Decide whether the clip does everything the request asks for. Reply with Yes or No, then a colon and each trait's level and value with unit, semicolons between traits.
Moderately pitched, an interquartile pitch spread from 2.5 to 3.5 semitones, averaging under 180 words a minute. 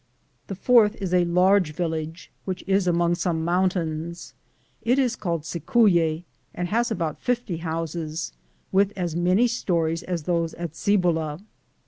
Yes: medium, 175 Hz; average, 3.1 semitones; average, 140 wpm